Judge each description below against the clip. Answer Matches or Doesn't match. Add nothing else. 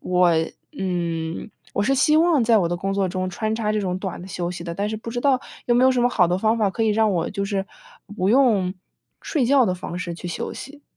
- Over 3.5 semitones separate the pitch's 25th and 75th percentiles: Matches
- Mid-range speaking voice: Doesn't match